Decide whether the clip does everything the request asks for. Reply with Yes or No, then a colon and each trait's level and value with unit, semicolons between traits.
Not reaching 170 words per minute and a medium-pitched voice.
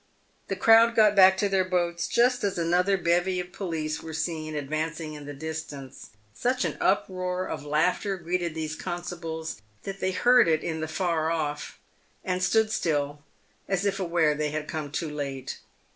No: average, 175 wpm; medium, 170 Hz